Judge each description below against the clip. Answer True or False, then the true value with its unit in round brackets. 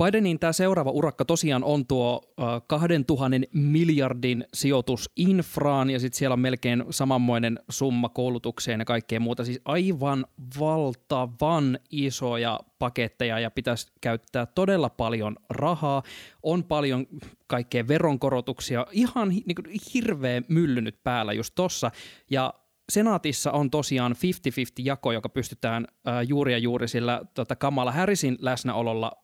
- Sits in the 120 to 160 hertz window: True (130 Hz)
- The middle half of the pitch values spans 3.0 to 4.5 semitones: True (3.9 semitones)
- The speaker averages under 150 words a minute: True (115 wpm)